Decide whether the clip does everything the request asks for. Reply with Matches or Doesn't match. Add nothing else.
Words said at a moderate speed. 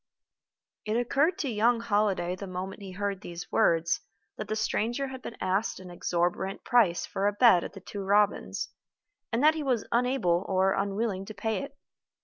Matches